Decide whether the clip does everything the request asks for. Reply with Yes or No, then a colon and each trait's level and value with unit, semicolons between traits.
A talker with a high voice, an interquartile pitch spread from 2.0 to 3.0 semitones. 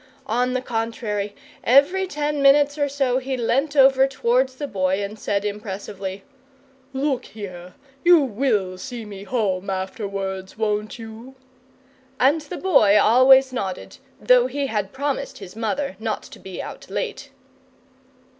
No: high, 235 Hz; average, 5.3 semitones